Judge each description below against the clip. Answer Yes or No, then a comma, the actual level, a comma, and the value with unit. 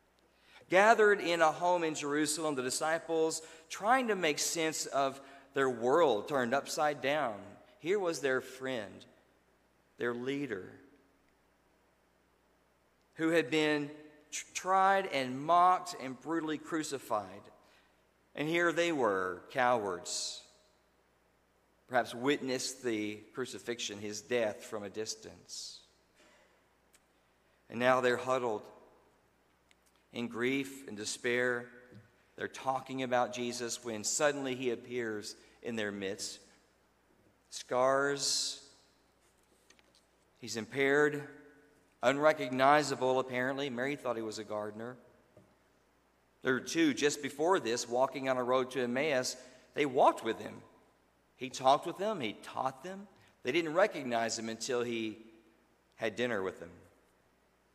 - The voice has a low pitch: Yes, low, 130 Hz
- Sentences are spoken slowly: Yes, slow, 115 wpm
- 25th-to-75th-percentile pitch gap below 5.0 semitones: Yes, average, 3.9 semitones